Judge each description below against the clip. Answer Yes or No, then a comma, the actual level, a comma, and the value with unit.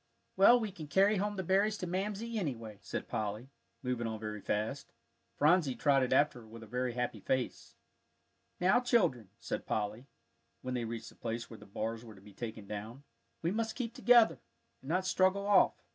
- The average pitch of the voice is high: No, low, 130 Hz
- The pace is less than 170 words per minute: No, average, 190 wpm